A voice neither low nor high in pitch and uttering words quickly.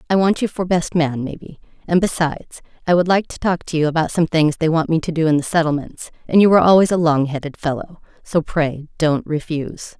Yes: medium, 165 Hz; fast, 235 wpm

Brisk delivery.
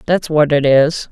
Yes: fast, 215 wpm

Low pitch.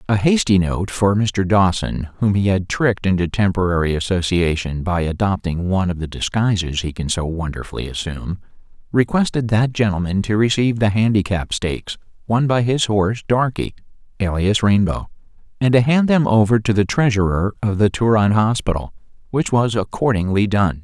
Yes: low, 100 Hz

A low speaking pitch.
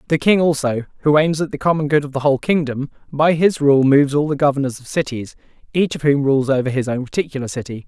No: medium, 145 Hz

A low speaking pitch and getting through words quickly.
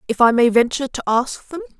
No: very high, 255 Hz; fast, 235 wpm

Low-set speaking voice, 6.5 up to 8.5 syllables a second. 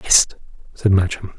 No: very low, 95 Hz; 4.2 syllables/s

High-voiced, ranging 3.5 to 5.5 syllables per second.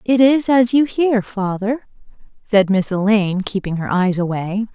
Yes: high, 210 Hz; 4.5 syllables/s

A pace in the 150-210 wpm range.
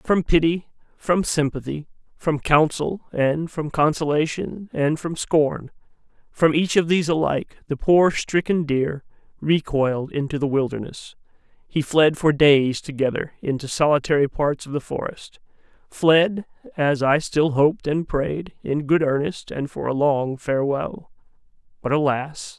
No: average, 140 wpm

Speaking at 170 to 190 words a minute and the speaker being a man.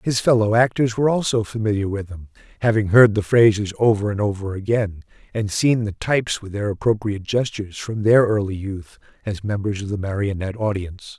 Yes: average, 180 wpm; male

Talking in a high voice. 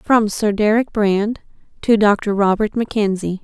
Yes: high, 210 Hz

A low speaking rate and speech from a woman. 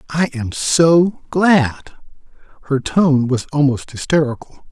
No: slow, 115 wpm; male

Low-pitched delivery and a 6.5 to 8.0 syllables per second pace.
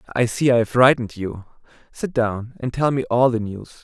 No: low, 120 Hz; 5.6 syllables/s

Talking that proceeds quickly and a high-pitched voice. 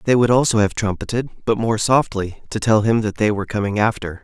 No: fast, 225 wpm; low, 110 Hz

